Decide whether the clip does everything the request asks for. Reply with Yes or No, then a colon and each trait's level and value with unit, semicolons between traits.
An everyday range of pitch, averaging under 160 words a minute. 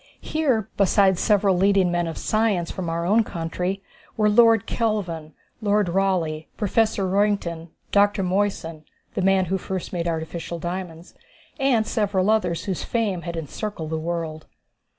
Yes: average, 3.5 semitones; average, 145 wpm